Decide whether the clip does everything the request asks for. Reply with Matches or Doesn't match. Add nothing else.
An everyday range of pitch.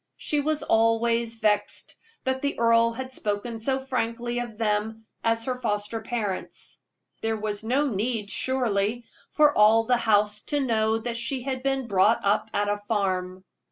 Matches